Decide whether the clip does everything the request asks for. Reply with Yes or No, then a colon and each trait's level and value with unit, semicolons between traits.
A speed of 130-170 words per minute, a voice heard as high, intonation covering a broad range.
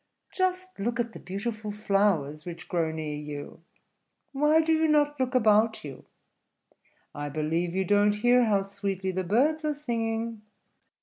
Yes: average, 150 wpm; high, 210 Hz; wide, 6.0 semitones